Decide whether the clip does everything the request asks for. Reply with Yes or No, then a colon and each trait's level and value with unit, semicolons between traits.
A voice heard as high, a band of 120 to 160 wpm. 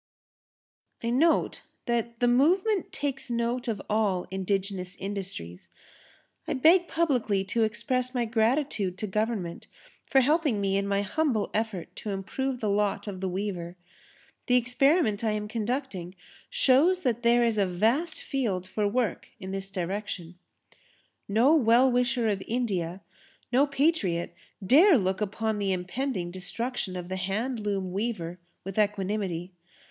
Yes: high, 215 Hz; average, 140 wpm